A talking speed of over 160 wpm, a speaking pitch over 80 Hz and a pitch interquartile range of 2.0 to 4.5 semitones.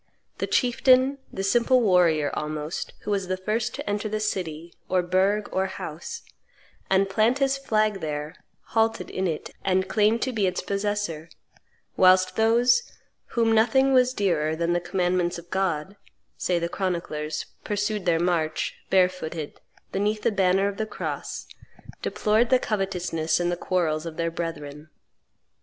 No: average, 150 wpm; high, 190 Hz; average, 4.1 semitones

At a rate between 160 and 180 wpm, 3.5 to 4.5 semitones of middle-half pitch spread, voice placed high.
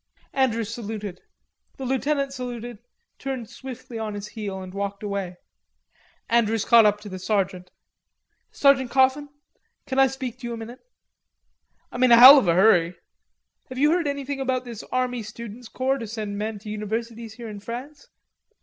Yes: average, 170 wpm; average, 3.8 semitones; high, 235 Hz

